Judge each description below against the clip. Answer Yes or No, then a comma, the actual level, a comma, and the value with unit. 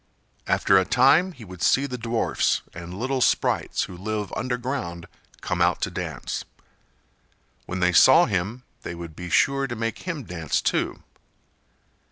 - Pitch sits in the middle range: No, low, 115 Hz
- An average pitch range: No, wide, 6.6 semitones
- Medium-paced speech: Yes, average, 155 wpm